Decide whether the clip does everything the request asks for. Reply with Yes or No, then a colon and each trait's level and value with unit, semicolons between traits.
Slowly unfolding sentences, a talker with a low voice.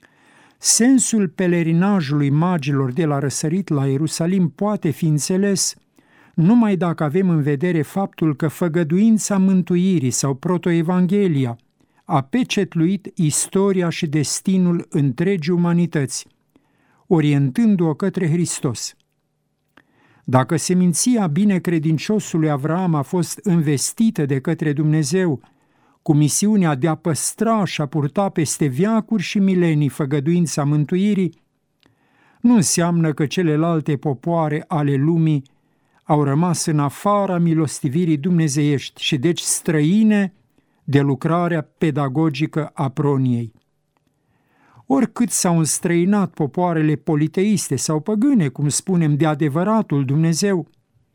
No: slow, 105 wpm; medium, 165 Hz